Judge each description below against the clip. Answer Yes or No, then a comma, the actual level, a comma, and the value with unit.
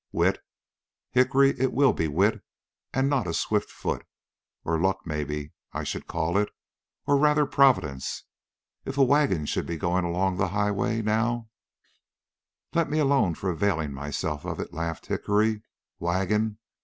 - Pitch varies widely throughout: Yes, wide, 7.6 semitones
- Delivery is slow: No, average, 155 wpm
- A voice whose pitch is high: No, low, 100 Hz